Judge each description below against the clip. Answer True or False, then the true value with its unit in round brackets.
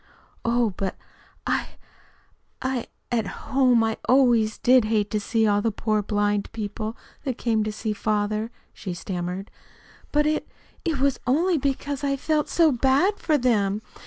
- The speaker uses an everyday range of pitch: True (4.3 semitones)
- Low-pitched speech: False (230 Hz)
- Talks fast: False (155 wpm)